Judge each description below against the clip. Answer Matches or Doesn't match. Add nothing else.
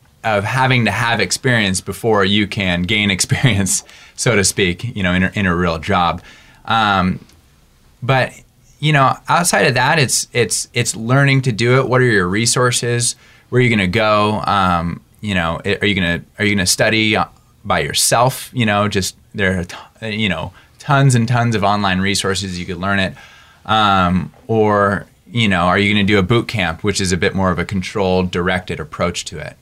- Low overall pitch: Matches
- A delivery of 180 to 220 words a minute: Matches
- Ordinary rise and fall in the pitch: Matches